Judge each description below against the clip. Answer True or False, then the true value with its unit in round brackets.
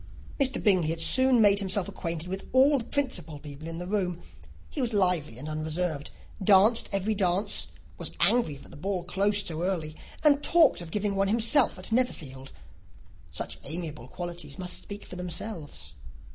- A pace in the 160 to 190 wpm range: True (170 wpm)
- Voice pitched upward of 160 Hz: True (185 Hz)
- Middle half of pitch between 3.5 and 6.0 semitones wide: True (4.9 semitones)